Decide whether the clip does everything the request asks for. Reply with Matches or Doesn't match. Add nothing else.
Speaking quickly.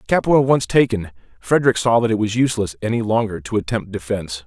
Doesn't match